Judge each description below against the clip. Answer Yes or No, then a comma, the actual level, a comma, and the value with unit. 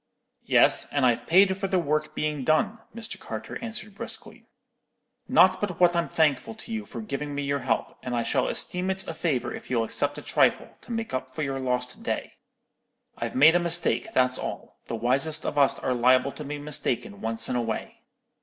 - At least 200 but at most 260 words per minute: Yes, fast, 205 wpm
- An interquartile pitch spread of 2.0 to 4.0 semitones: No, wide, 5.6 semitones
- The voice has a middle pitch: Yes, medium, 145 Hz